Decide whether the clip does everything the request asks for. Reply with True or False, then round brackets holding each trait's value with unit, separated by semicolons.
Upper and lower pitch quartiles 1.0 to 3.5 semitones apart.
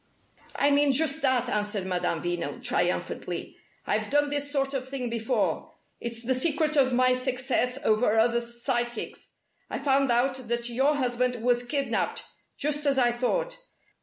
True (2.8 semitones)